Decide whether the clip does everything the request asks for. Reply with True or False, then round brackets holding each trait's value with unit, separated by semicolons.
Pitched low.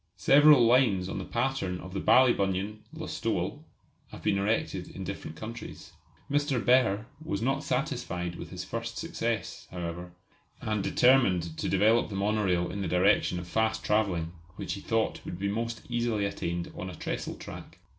True (105 Hz)